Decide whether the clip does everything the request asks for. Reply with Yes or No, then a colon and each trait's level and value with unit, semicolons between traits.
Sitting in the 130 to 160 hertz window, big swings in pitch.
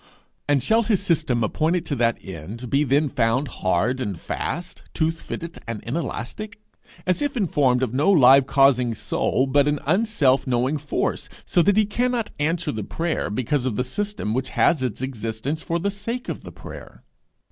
Yes: medium, 140 Hz; wide, 5.9 semitones